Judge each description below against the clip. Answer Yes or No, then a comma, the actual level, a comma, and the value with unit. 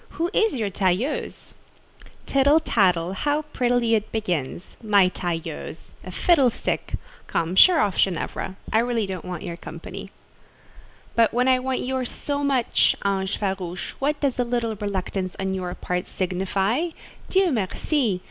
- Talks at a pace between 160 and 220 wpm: No, average, 140 wpm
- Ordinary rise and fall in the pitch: No, wide, 5.9 semitones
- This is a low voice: No, high, 215 Hz